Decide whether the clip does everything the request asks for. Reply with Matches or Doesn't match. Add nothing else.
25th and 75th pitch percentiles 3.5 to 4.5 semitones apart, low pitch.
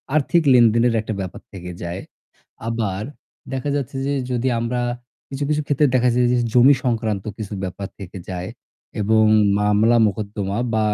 Matches